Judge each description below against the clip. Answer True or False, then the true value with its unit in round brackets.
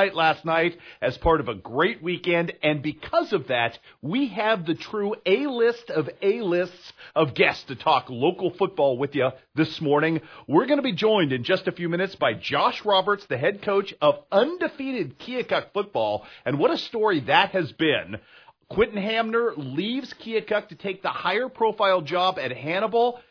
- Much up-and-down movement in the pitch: True (5.8 semitones)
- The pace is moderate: True (170 wpm)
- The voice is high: True (195 Hz)